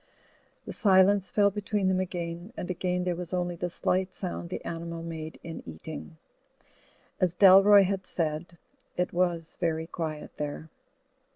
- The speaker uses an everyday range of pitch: No, narrow, 2.1 semitones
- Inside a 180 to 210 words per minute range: No, average, 150 wpm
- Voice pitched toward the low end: No, medium, 175 Hz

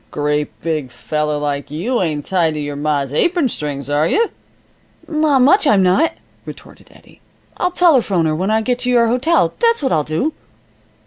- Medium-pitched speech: Yes, medium, 180 Hz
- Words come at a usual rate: Yes, average, 185 wpm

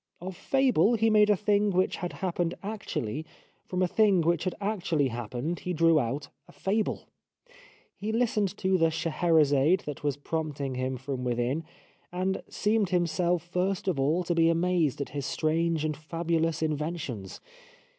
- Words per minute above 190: No, average, 160 wpm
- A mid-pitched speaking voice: Yes, medium, 170 Hz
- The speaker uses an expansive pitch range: No, average, 4.1 semitones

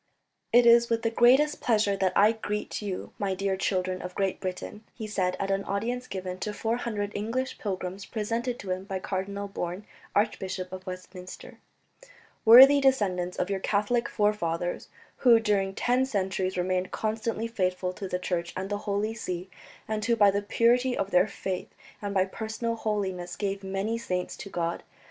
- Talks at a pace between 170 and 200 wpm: Yes, average, 175 wpm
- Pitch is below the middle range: No, high, 200 Hz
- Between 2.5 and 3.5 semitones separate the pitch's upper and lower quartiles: Yes, average, 3.2 semitones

